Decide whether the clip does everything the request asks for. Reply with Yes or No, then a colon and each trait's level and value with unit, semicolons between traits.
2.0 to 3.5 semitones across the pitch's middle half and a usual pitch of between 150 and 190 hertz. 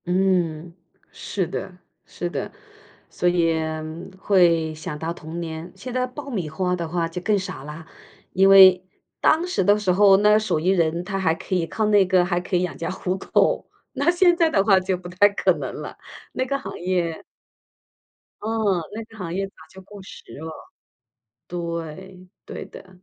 Yes: average, 3.0 semitones; medium, 185 Hz